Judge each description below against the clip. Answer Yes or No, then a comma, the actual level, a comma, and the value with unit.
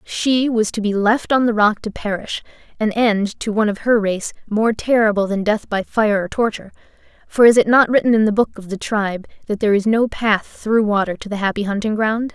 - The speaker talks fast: Yes, fast, 235 wpm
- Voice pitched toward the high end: Yes, high, 215 Hz